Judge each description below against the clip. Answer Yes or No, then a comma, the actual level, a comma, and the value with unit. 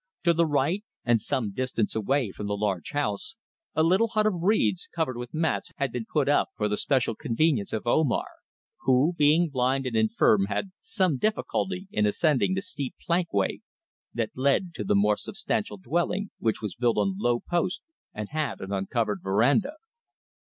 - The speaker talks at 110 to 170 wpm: No, average, 180 wpm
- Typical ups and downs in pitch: No, wide, 7.6 semitones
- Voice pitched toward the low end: Yes, low, 130 Hz